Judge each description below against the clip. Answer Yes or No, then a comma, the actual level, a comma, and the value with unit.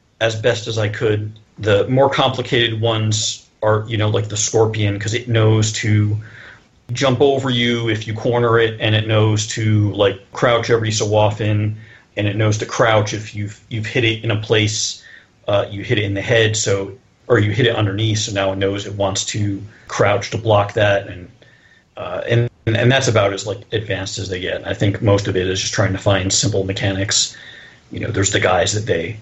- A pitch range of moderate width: No, narrow, 2.1 semitones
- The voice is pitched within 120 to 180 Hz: No, low, 110 Hz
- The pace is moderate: No, fast, 210 wpm